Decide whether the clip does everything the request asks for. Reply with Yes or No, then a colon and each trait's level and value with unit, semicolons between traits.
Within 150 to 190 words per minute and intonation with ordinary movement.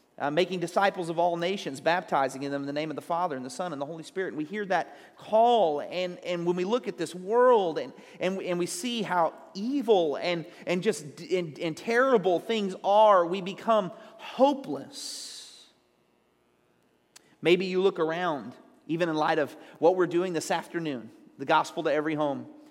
Yes: average, 180 wpm; average, 3.7 semitones